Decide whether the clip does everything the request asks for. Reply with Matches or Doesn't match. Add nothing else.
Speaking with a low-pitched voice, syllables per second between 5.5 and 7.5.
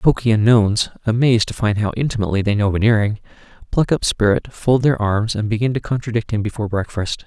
Matches